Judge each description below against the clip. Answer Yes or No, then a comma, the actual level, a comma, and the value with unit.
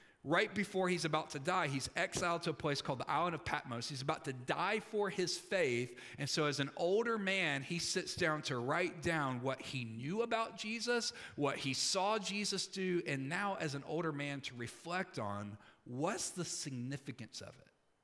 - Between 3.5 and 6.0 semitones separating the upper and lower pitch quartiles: Yes, average, 5.2 semitones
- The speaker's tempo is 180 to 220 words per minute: Yes, average, 195 wpm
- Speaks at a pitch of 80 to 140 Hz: No, medium, 160 Hz